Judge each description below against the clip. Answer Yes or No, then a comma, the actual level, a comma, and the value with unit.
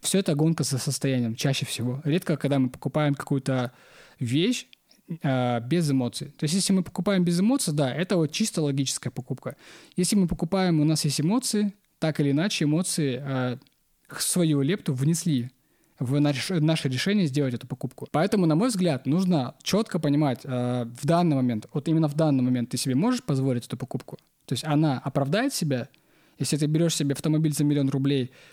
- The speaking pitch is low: No, medium, 150 Hz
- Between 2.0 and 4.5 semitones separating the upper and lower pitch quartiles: Yes, average, 4.2 semitones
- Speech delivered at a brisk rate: Yes, fast, 180 wpm